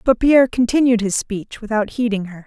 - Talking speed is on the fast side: No, average, 195 wpm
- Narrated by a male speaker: No, female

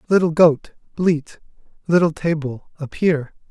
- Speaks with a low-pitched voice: No, medium, 160 Hz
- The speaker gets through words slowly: Yes, slow, 105 wpm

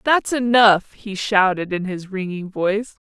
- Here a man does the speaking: No, female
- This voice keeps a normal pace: Yes, average, 155 wpm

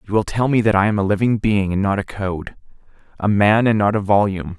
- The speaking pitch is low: Yes, low, 100 Hz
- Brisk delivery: Yes, fast, 250 wpm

